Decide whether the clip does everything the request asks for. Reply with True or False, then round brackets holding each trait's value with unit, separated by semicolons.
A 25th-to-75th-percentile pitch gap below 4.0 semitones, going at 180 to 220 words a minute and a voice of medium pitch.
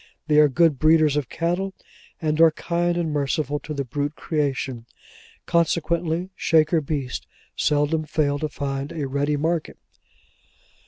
False (2.4 semitones; 140 wpm; 155 Hz)